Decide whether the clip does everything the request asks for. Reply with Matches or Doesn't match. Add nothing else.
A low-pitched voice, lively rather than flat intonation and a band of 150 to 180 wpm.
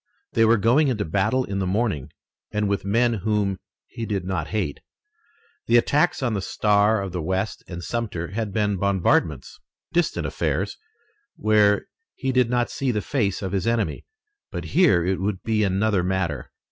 Doesn't match